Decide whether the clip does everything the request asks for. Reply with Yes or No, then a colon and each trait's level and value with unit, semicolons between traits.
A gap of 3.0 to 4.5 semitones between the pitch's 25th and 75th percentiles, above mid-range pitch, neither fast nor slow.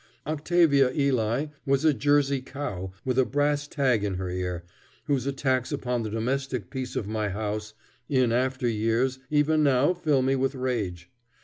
No: average, 4.2 semitones; low, 130 Hz; average, 165 wpm